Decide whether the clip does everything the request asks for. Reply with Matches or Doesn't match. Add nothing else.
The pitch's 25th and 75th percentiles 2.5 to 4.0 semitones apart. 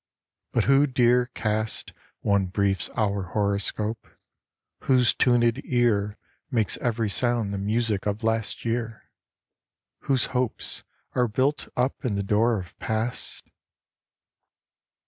Matches